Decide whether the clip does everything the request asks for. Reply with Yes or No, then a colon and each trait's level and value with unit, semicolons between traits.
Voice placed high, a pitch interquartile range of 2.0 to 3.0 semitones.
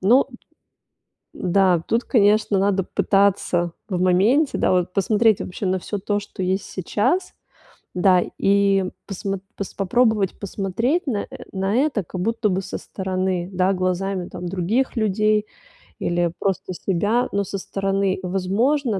Yes: high, 195 Hz; narrow, 2.4 semitones